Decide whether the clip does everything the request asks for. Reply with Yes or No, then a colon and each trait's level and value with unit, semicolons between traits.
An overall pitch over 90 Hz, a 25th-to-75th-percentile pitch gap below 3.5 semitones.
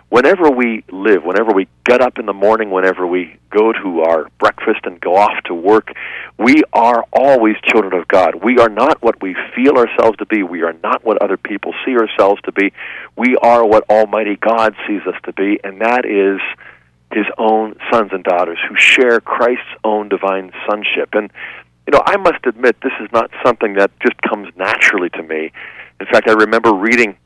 Yes: low, 105 Hz; average, 2.8 semitones